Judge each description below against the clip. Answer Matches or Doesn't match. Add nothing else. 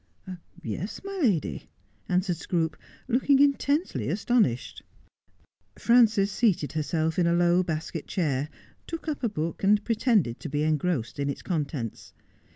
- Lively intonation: Matches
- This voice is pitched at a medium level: Matches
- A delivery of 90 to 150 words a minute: Matches